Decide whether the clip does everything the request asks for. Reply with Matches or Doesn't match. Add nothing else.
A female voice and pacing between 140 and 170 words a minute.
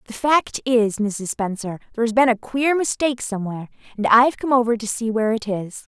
Doesn't match